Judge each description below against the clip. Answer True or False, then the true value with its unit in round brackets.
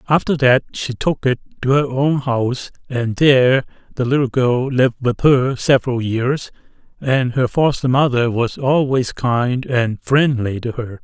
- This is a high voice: False (130 Hz)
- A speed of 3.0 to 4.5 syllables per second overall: True (4.3 syllables/s)